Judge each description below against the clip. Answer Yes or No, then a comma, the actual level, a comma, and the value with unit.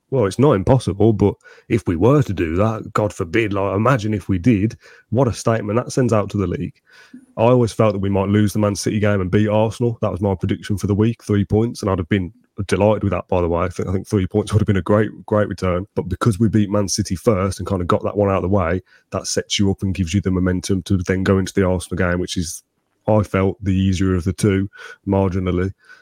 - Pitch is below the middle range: Yes, low, 100 Hz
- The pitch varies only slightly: Yes, narrow, 2.1 semitones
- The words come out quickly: Yes, fast, 270 wpm